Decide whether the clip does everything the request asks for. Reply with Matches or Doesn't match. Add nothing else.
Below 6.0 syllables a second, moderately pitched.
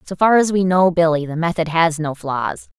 Matches